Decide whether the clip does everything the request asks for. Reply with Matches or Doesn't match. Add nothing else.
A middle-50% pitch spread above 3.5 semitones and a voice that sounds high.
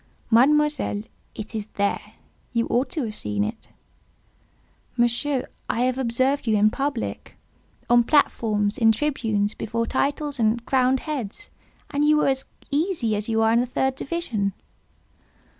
Matches